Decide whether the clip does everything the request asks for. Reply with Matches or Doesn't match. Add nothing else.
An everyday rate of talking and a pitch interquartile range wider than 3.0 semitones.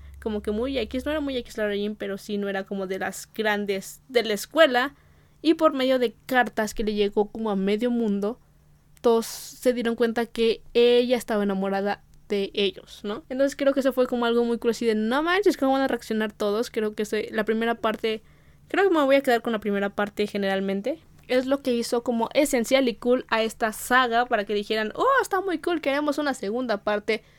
Doesn't match